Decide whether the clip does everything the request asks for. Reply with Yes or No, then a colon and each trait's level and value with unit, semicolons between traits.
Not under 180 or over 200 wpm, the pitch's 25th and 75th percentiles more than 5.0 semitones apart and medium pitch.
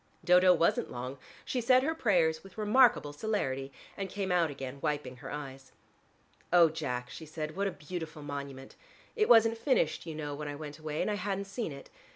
Yes: average, 195 wpm; wide, 5.6 semitones; medium, 160 Hz